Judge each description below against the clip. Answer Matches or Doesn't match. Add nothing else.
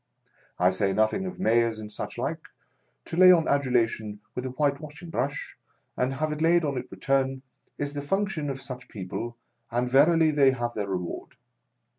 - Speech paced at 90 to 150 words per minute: Doesn't match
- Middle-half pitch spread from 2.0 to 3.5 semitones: Doesn't match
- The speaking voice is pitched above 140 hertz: Doesn't match